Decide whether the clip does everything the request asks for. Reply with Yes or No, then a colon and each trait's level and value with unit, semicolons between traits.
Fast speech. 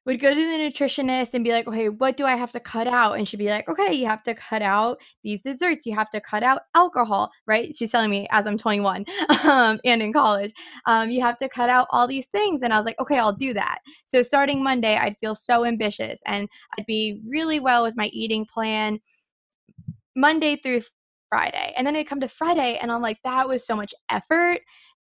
Yes: fast, 230 wpm